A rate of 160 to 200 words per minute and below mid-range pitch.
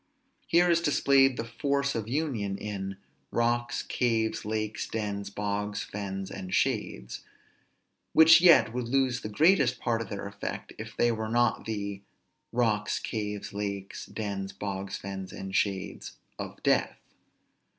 No: average, 140 wpm; low, 110 Hz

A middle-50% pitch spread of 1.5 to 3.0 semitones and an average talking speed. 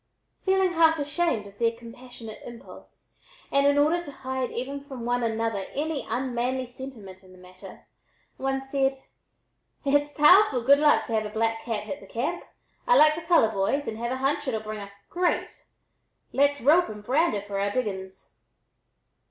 No: average, 4.7 semitones; average, 175 wpm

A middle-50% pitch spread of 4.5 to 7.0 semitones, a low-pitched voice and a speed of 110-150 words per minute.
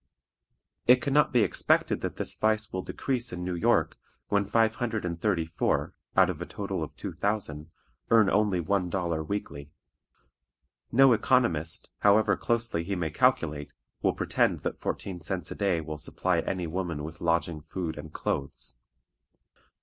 No: average, 5.0 semitones; very low, 90 Hz; average, 165 wpm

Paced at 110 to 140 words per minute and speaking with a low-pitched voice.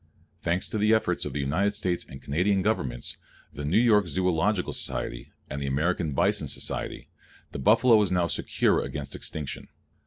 No: average, 165 wpm; very low, 90 Hz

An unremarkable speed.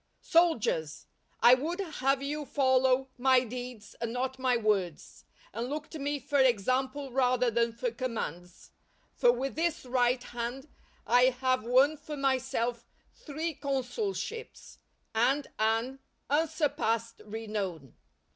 No: slow, 125 wpm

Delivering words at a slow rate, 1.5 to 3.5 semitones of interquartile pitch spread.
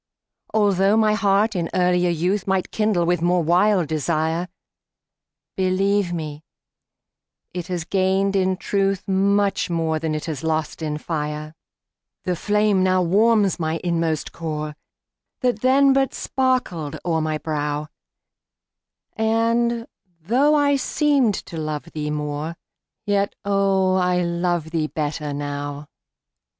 No: slow, 125 wpm; average, 4.3 semitones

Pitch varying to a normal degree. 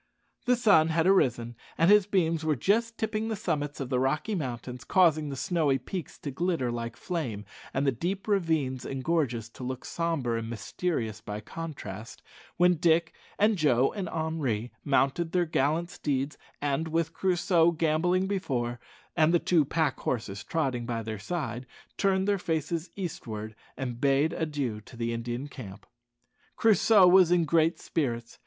No: wide, 5.8 semitones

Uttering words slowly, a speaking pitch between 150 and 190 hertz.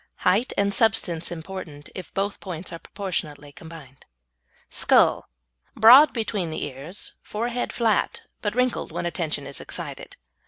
Yes: slow, 130 wpm; medium, 185 Hz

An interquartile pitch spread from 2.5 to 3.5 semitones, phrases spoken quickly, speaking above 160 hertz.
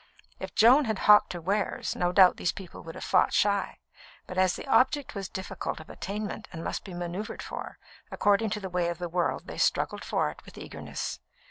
Yes: average, 2.9 semitones; fast, 210 wpm; high, 190 Hz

